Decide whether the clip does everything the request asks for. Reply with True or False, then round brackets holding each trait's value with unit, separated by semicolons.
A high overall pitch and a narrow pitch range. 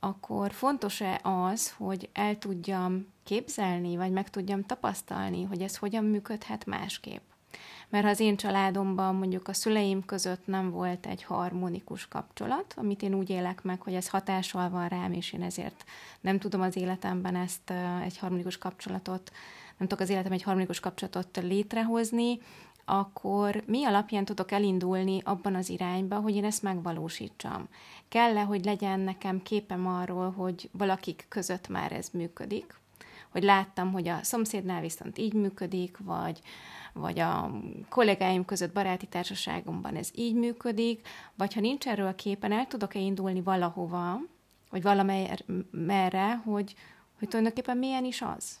True (195 Hz; 2.0 semitones)